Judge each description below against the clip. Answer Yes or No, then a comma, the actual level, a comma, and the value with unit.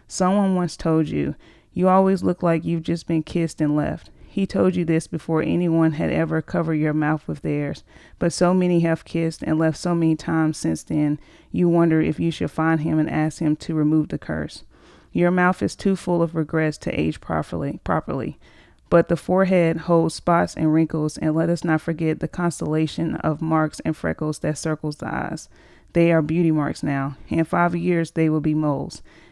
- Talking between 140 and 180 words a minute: No, average, 200 wpm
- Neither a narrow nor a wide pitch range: No, narrow, 1.6 semitones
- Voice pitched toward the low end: No, medium, 160 Hz